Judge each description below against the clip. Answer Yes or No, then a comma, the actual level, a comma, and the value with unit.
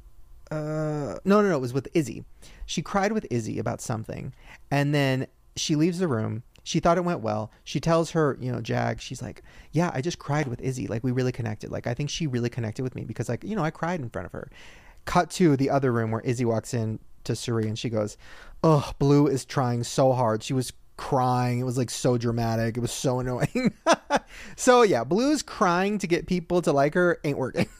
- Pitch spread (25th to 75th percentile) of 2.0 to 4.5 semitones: No, average, 5.3 semitones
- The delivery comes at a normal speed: No, fast, 225 wpm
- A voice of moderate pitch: No, low, 130 Hz